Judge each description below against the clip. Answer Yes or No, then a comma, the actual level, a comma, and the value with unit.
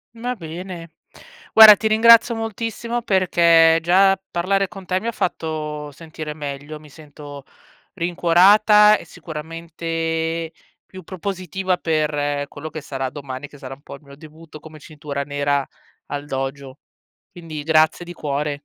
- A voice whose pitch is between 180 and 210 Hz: No, medium, 160 Hz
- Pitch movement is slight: No, average, 4.2 semitones